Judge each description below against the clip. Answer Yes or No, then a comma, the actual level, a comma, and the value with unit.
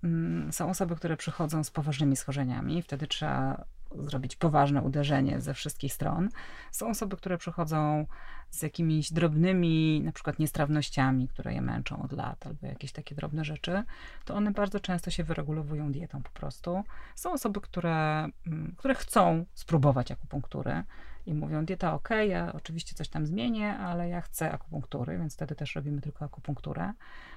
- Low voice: No, medium, 155 Hz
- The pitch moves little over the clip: No, average, 3.3 semitones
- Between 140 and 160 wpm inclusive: Yes, average, 155 wpm